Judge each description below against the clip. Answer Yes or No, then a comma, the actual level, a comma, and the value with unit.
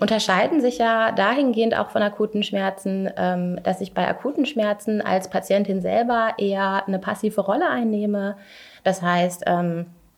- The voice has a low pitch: No, high, 205 Hz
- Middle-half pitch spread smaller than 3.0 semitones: Yes, narrow, 2.5 semitones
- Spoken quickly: No, average, 135 wpm